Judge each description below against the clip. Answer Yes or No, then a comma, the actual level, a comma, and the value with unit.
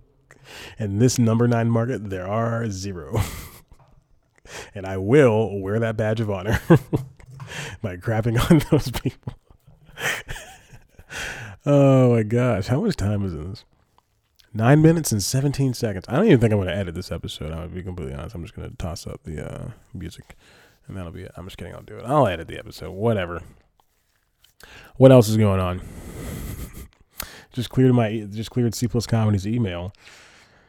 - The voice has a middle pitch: No, low, 110 Hz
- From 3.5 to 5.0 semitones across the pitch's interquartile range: Yes, average, 4.7 semitones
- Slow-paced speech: No, average, 165 wpm